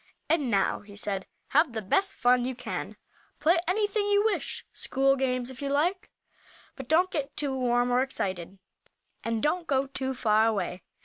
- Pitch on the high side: Yes, very high, 265 Hz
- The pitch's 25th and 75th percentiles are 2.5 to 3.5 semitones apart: No, average, 5.2 semitones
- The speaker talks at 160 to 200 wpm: Yes, average, 175 wpm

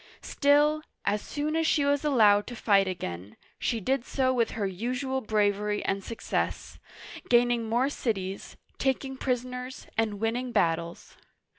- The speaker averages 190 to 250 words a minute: No, average, 145 wpm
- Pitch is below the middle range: No, high, 235 Hz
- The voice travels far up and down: No, average, 4.4 semitones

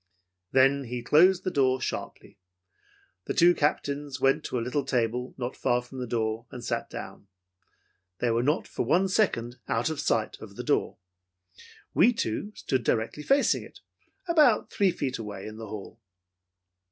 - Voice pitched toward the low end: Yes, low, 130 Hz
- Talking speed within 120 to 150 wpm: No, average, 165 wpm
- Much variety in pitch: No, average, 4.6 semitones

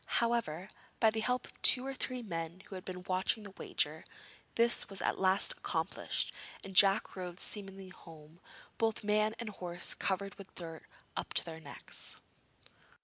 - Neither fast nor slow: Yes, average, 165 wpm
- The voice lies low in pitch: No, high, 195 Hz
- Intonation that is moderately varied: Yes, average, 3.7 semitones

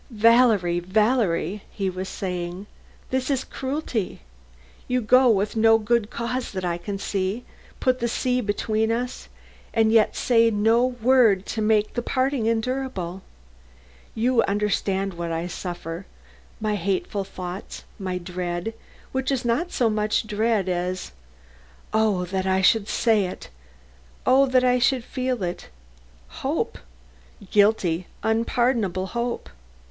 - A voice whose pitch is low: No, high, 215 Hz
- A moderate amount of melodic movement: Yes, average, 4.3 semitones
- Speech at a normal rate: No, slow, 130 wpm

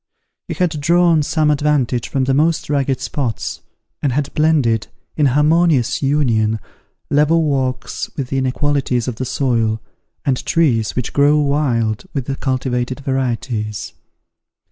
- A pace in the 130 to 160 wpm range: Yes, slow, 135 wpm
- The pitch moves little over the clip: No, average, 3.3 semitones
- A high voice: No, low, 135 Hz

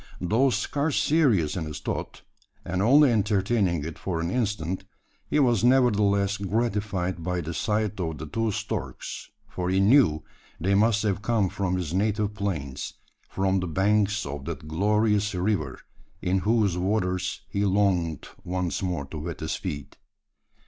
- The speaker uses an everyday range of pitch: Yes, average, 3.3 semitones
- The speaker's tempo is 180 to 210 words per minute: No, average, 155 wpm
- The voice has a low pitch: Yes, very low, 95 Hz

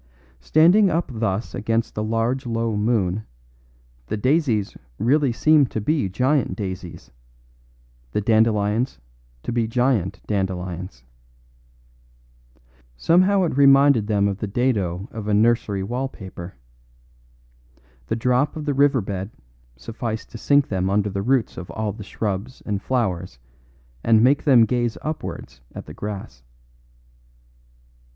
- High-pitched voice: No, low, 110 Hz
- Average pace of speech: No, slow, 130 wpm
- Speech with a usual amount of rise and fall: Yes, average, 4.9 semitones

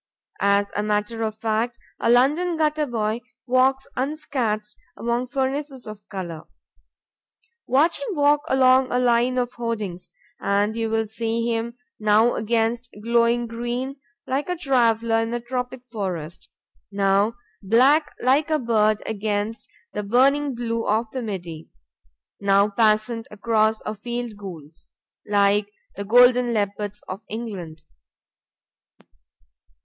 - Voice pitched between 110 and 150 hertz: No, high, 230 Hz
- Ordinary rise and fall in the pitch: Yes, average, 3.1 semitones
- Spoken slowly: Yes, slow, 125 wpm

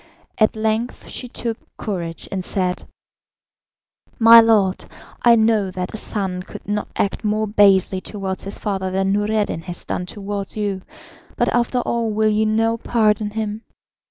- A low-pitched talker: No, high, 210 Hz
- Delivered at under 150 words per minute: No, average, 155 wpm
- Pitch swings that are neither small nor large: No, narrow, 2.3 semitones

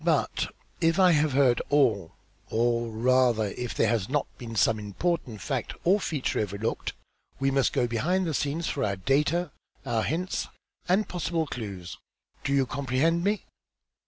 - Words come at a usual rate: Yes, average, 160 wpm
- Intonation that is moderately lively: No, wide, 6.3 semitones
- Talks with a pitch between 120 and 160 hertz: Yes, low, 135 Hz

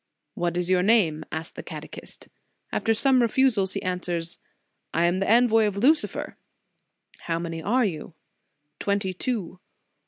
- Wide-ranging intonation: No, average, 4.7 semitones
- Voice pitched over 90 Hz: Yes, high, 190 Hz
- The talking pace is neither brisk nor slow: Yes, average, 150 wpm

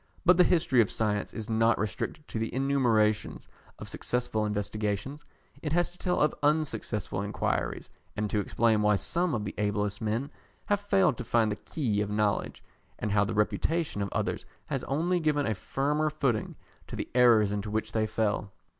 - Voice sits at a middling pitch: No, low, 110 Hz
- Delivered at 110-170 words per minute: No, average, 180 wpm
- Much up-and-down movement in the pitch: Yes, wide, 5.9 semitones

